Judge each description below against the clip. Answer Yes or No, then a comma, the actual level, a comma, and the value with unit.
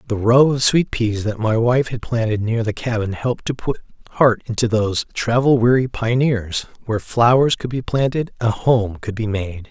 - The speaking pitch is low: Yes, low, 115 Hz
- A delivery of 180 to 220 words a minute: Yes, average, 200 wpm